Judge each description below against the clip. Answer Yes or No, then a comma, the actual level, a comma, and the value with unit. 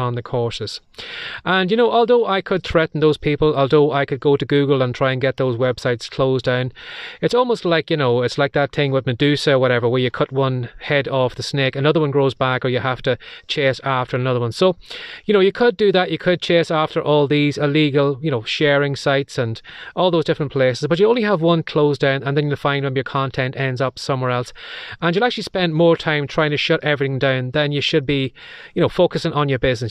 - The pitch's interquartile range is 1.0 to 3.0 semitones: No, average, 3.7 semitones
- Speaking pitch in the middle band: Yes, medium, 145 Hz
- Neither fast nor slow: No, fast, 245 wpm